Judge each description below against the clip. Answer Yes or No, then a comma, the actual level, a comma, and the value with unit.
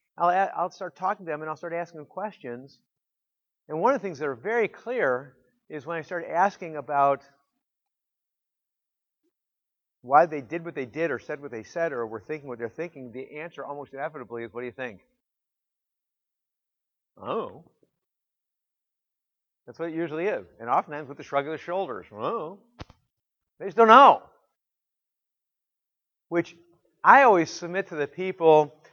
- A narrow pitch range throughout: No, average, 3.7 semitones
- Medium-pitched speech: Yes, medium, 155 Hz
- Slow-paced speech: No, average, 165 wpm